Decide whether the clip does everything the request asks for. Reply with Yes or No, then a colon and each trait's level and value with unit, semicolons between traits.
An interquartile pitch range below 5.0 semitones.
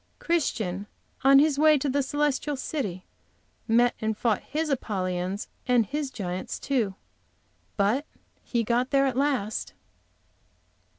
No: wide, 5.5 semitones